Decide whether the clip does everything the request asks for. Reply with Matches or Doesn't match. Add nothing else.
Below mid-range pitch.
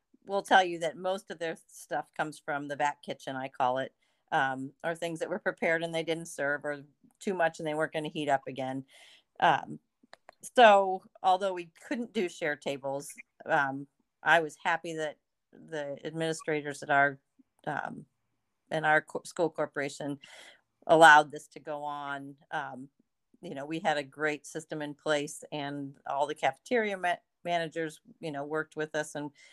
Doesn't match